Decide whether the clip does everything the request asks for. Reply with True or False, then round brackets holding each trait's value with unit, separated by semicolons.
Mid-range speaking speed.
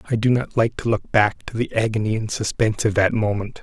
False (250 wpm)